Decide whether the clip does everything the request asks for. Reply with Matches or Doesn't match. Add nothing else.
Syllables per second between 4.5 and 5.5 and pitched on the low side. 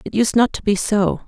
Doesn't match